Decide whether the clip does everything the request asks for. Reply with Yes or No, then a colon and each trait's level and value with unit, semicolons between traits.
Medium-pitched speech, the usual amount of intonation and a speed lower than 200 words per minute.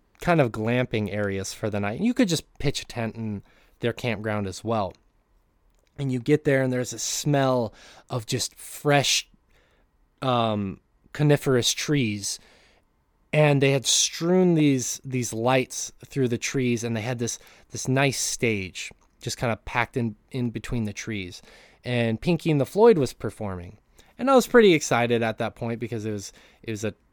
No: low, 120 Hz; average, 3.9 semitones; average, 175 wpm